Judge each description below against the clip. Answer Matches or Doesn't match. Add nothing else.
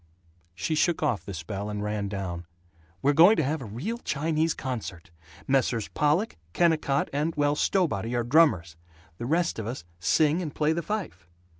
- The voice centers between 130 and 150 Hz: Matches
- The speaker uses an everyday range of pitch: Doesn't match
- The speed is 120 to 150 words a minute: Doesn't match